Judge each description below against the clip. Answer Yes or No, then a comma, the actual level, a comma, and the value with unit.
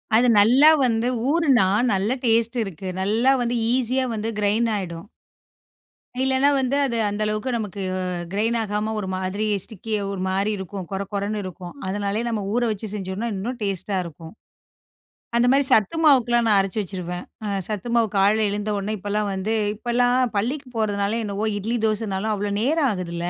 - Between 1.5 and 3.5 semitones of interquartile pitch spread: Yes, average, 3.2 semitones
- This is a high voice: Yes, high, 210 Hz